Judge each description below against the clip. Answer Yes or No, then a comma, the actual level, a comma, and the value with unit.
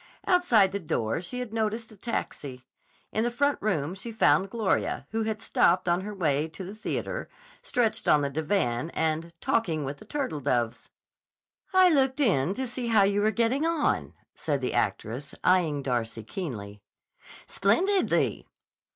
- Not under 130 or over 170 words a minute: Yes, average, 160 wpm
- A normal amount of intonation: No, wide, 7.9 semitones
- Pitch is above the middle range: Yes, high, 195 Hz